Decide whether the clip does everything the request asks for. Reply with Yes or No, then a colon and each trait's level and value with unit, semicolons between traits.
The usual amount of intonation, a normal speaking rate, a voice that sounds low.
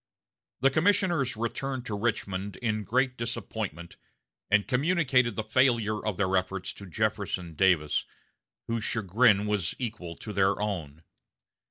No: average, 4.4 semitones; slow, 130 wpm; low, 105 Hz